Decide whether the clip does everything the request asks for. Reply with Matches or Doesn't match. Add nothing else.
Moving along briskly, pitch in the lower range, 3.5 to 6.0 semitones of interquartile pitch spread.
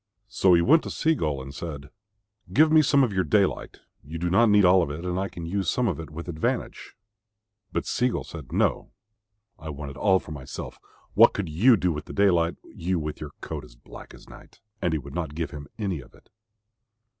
Matches